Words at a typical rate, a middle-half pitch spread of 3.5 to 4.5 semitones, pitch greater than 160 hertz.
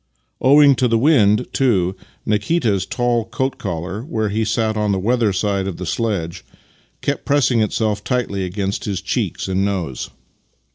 No: average, 155 wpm; average, 3.9 semitones; low, 105 Hz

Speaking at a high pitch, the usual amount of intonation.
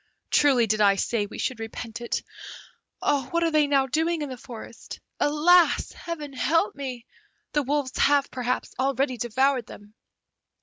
Yes: very high, 265 Hz; average, 3.6 semitones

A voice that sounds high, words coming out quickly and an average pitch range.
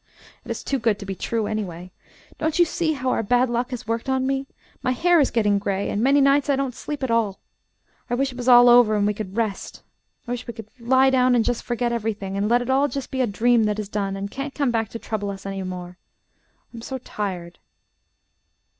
Yes: high, 235 Hz; fast, 245 wpm; average, 4.1 semitones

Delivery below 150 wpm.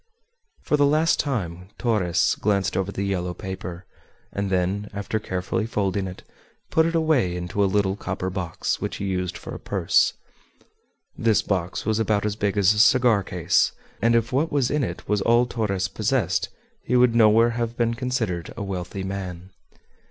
No: average, 175 wpm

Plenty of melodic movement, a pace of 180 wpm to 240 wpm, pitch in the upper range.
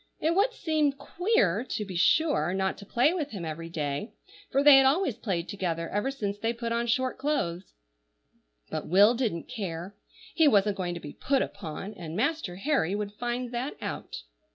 Yes: wide, 7.2 semitones; average, 185 wpm; high, 215 Hz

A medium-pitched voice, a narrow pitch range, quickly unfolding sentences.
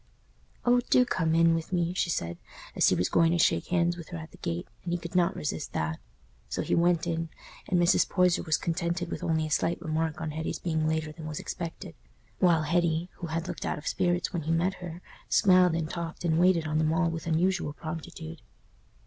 Yes: medium, 165 Hz; narrow, 1.7 semitones; fast, 220 wpm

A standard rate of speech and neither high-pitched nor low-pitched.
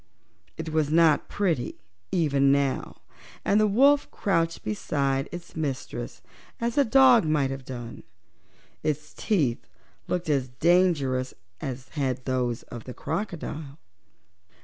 No: slow, 125 wpm; medium, 150 Hz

